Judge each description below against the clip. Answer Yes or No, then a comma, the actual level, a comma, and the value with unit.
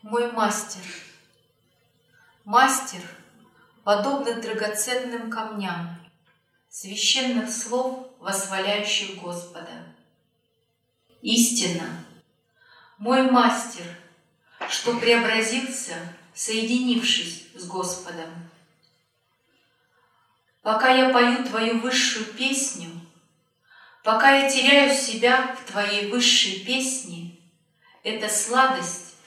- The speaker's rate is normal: No, slow, 70 wpm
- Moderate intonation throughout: No, wide, 6.2 semitones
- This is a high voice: Yes, high, 215 Hz